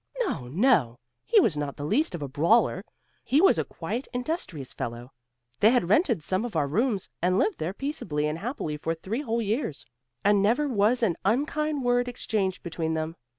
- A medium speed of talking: Yes, average, 190 wpm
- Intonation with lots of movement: Yes, wide, 7.7 semitones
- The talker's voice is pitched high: Yes, high, 205 Hz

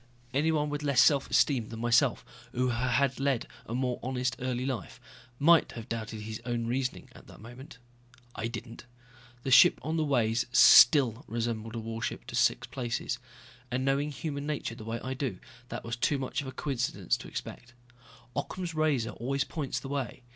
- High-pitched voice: No, low, 125 Hz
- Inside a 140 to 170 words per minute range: No, average, 185 wpm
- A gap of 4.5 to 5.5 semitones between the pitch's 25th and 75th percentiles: No, average, 3.2 semitones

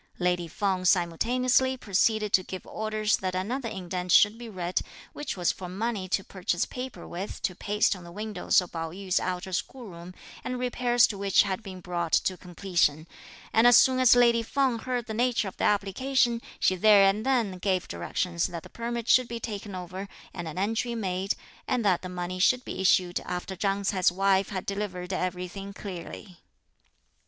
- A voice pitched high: Yes, high, 195 Hz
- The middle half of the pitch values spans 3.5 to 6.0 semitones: Yes, average, 4.0 semitones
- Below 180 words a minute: No, average, 185 wpm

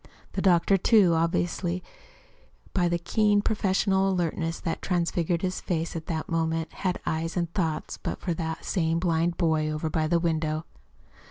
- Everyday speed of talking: Yes, average, 160 wpm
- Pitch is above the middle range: No, medium, 170 Hz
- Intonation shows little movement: Yes, narrow, 2.1 semitones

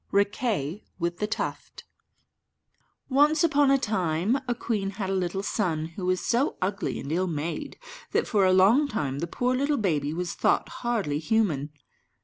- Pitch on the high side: Yes, high, 195 Hz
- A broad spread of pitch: Yes, wide, 6.0 semitones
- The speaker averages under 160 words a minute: No, average, 165 wpm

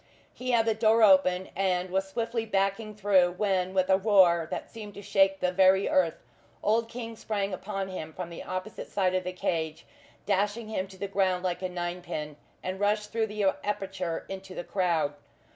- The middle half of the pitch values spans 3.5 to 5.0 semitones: No, narrow, 2.4 semitones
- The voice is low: No, high, 190 Hz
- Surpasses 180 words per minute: Yes, average, 190 wpm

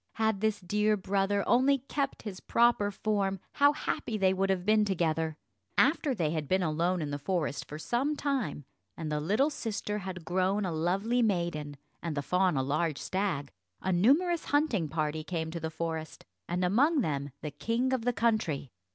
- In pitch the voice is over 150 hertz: Yes, high, 190 Hz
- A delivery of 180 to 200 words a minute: Yes, average, 185 wpm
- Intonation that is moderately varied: No, wide, 5.8 semitones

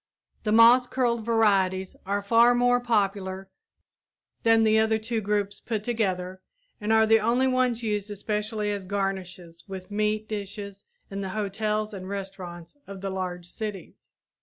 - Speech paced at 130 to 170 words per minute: Yes, average, 150 wpm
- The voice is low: No, high, 210 Hz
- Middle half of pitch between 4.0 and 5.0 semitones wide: No, narrow, 2.5 semitones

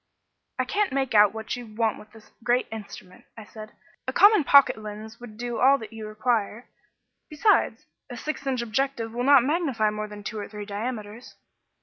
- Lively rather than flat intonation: No, average, 3.6 semitones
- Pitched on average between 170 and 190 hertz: No, high, 225 Hz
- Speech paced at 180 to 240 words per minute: Yes, average, 190 wpm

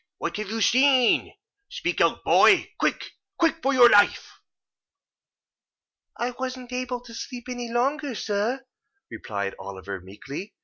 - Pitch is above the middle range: Yes, high, 240 Hz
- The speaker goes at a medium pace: No, slow, 125 wpm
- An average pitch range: Yes, average, 3.9 semitones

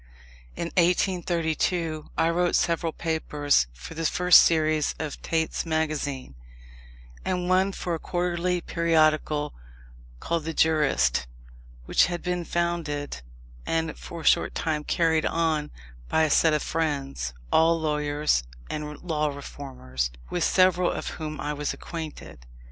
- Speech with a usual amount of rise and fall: No, narrow, 2.3 semitones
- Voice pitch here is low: No, medium, 160 Hz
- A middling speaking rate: No, slow, 130 wpm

